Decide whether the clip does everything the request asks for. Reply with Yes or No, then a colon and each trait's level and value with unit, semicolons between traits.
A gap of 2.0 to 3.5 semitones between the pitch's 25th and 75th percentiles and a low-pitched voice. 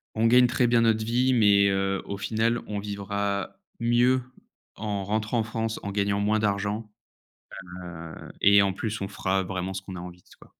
Yes: narrow, 2.5 semitones; low, 100 Hz